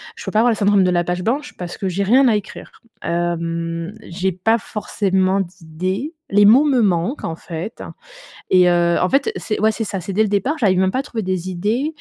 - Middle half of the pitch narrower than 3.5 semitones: No, average, 4.0 semitones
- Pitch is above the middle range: Yes, high, 195 Hz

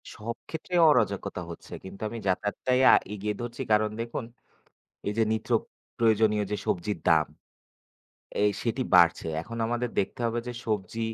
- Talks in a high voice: No, low, 110 Hz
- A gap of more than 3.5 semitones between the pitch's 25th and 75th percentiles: No, narrow, 2.4 semitones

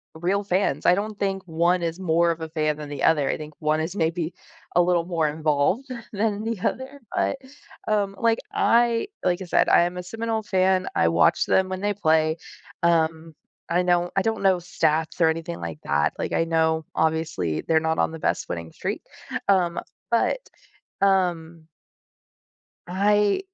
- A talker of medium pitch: Yes, medium, 175 Hz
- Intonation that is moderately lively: Yes, average, 3.6 semitones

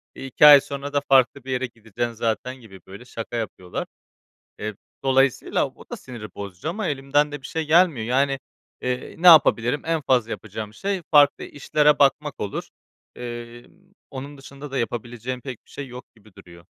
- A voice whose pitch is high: No, low, 130 Hz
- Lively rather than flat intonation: No, average, 3.7 semitones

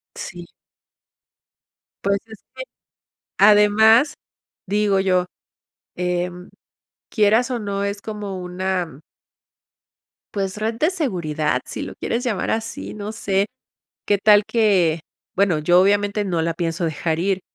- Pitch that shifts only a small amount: No, average, 3.0 semitones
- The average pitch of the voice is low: No, high, 200 Hz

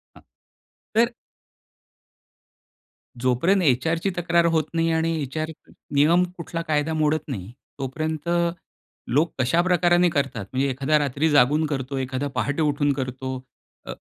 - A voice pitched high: No, medium, 150 Hz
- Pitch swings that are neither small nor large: Yes, average, 3.6 semitones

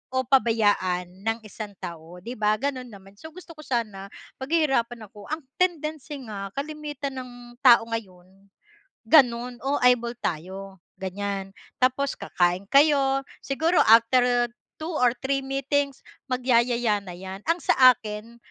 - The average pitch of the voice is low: No, high, 240 Hz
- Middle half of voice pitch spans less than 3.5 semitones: No, average, 5.3 semitones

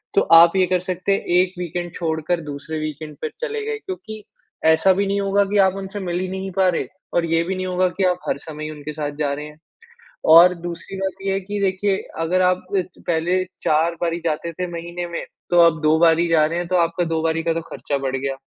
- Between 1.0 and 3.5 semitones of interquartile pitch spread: Yes, average, 2.7 semitones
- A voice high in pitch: No, medium, 175 Hz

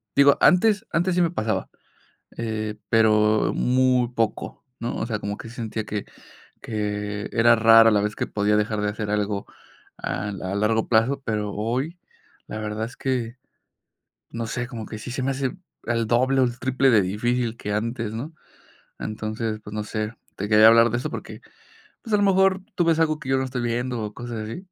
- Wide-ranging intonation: No, average, 3.2 semitones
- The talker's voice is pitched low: Yes, low, 115 Hz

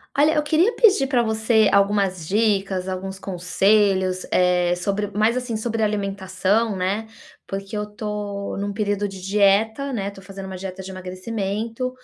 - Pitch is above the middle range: Yes, high, 200 Hz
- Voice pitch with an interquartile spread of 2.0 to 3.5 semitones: Yes, narrow, 2.5 semitones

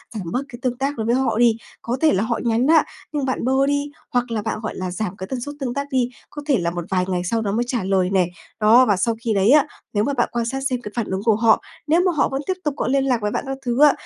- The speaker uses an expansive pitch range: No, average, 4.4 semitones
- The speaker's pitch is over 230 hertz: Yes, high, 240 Hz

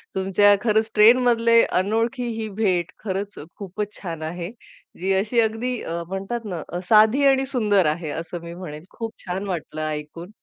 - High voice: Yes, high, 205 Hz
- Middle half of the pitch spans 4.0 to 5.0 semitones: Yes, average, 4.4 semitones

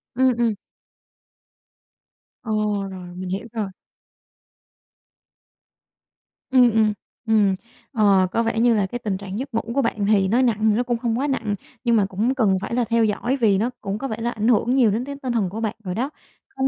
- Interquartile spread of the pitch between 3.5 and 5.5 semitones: No, average, 3.0 semitones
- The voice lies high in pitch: Yes, high, 225 Hz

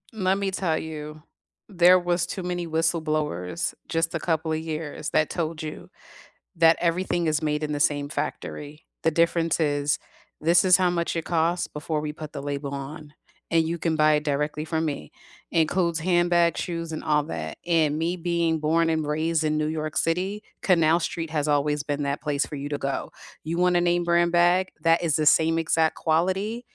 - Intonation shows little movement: Yes, narrow, 2.2 semitones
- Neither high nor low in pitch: Yes, medium, 160 Hz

